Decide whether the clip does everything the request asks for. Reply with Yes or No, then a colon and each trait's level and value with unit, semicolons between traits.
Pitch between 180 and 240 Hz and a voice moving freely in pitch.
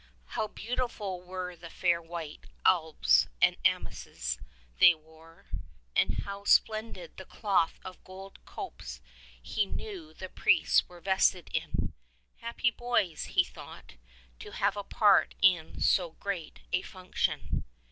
No: medium, 185 Hz; average, 3.6 semitones